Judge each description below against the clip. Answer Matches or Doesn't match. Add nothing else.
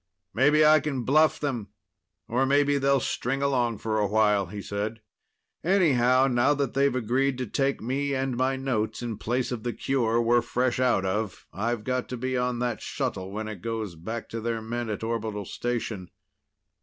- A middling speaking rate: Matches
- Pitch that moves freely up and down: Doesn't match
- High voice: Doesn't match